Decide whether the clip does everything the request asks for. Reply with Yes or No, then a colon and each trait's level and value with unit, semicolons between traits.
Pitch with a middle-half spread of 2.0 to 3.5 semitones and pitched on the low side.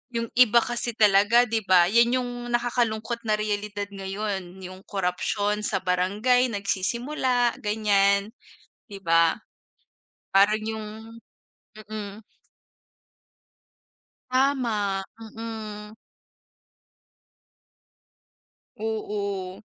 No: average, 2.7 semitones; high, 210 Hz